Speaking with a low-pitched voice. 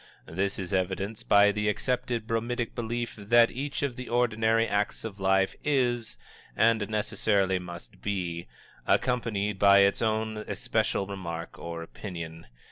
Yes: low, 105 Hz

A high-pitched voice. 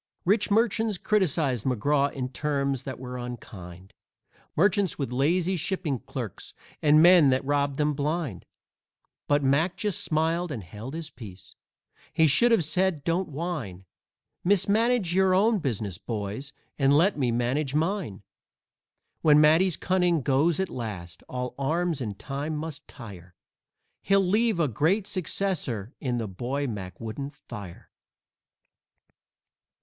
No: medium, 145 Hz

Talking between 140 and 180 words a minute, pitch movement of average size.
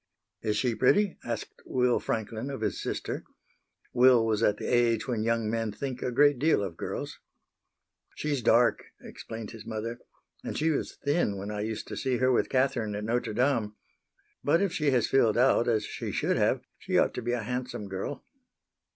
No: average, 190 wpm; average, 3.1 semitones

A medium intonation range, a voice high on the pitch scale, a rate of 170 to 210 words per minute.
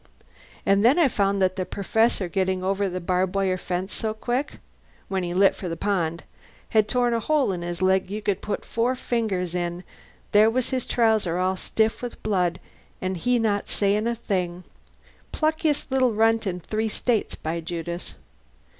Yes: average, 3.8 semitones; high, 200 Hz; average, 180 wpm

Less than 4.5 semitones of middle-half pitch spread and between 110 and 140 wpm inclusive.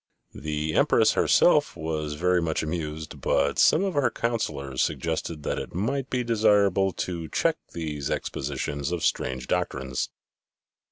No: average, 5.2 semitones; slow, 135 wpm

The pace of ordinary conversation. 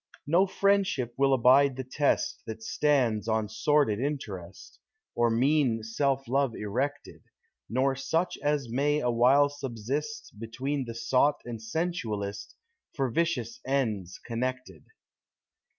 No: slow, 120 wpm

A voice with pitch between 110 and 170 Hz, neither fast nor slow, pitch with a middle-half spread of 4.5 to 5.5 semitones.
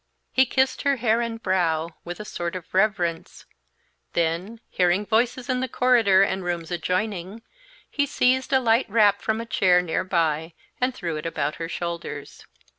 No: high, 195 Hz; average, 170 wpm; average, 5.2 semitones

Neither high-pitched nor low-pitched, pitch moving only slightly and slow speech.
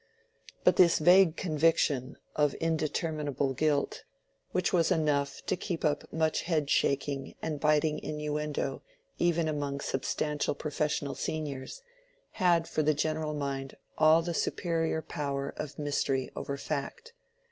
Yes: medium, 150 Hz; narrow, 2.3 semitones; slow, 125 wpm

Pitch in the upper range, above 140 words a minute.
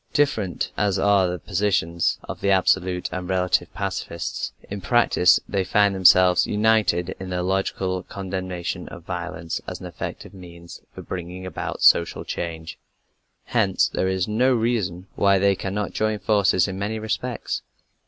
No: very low, 95 Hz; average, 155 wpm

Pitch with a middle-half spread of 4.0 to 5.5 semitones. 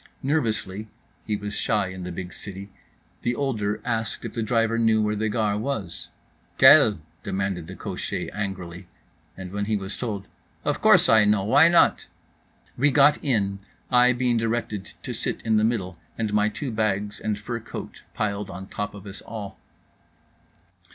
No: narrow, 2.6 semitones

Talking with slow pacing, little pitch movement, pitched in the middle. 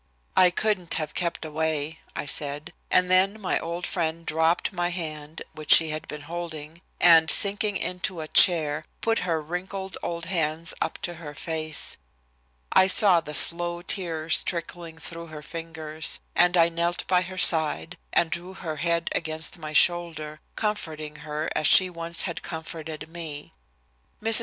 No: average, 160 wpm; narrow, 2.2 semitones; medium, 165 Hz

